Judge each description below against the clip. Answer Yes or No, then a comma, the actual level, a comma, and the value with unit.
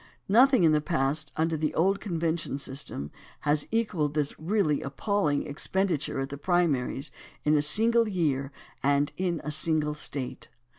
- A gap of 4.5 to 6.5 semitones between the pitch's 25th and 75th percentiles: No, average, 4.0 semitones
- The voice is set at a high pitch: No, medium, 155 Hz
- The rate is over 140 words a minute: Yes, average, 150 wpm